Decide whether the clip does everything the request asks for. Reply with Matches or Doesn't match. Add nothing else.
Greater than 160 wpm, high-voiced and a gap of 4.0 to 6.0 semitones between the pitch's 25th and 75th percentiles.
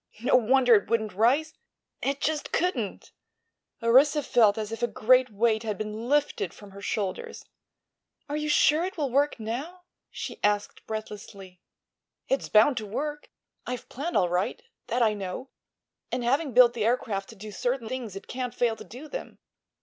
Matches